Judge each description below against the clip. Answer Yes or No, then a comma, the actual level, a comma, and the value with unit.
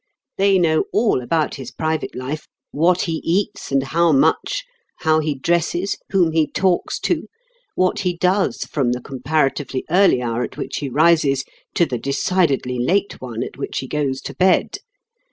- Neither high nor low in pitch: Yes, medium, 155 Hz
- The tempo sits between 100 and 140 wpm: No, average, 170 wpm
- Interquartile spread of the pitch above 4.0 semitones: Yes, average, 4.8 semitones